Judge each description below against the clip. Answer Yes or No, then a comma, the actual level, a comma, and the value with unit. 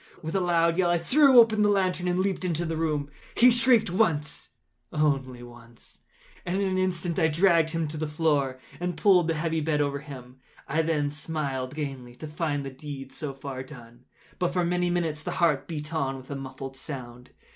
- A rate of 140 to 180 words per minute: No, average, 195 wpm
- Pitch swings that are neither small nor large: Yes, average, 4.4 semitones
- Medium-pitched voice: Yes, medium, 155 Hz